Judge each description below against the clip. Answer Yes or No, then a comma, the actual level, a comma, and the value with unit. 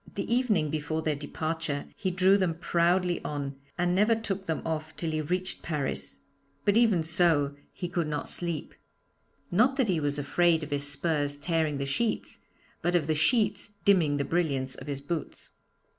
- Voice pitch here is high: No, medium, 165 Hz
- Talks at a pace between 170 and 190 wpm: Yes, average, 175 wpm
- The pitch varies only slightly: No, average, 3.9 semitones